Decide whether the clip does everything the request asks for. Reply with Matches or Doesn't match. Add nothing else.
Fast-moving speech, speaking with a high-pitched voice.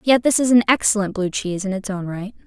Matches